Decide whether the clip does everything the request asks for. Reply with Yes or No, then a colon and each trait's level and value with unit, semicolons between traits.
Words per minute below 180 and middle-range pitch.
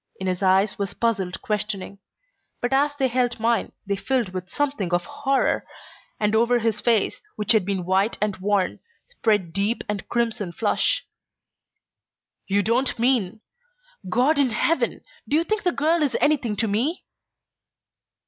No: average, 155 wpm; high, 220 Hz